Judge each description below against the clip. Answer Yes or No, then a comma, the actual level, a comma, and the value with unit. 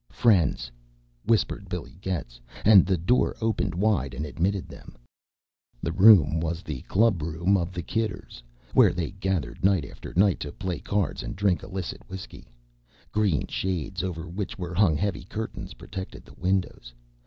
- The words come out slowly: No, average, 155 wpm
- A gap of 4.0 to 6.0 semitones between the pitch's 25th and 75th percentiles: No, average, 3.2 semitones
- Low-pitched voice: Yes, very low, 95 Hz